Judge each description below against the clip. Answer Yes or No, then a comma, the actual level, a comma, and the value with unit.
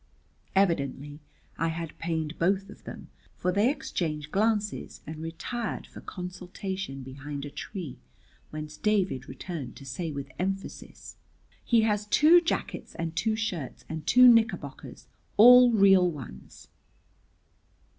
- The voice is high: No, medium, 180 Hz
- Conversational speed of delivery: No, slow, 125 wpm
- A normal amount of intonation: No, wide, 5.7 semitones